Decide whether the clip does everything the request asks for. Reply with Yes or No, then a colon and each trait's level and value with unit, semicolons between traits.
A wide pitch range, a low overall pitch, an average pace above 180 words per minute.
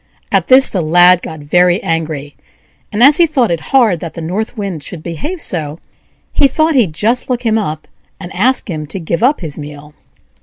No: wide, 7.5 semitones; medium, 180 Hz; average, 200 wpm